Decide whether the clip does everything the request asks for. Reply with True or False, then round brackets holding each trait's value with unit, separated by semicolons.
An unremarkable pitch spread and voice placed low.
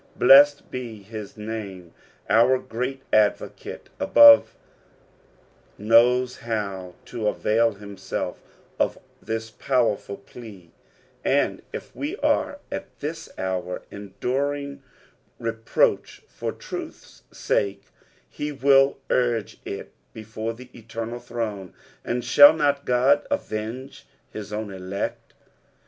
True (3.4 semitones; 115 Hz)